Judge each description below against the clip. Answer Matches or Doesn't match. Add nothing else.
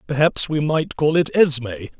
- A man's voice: Matches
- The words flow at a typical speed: Matches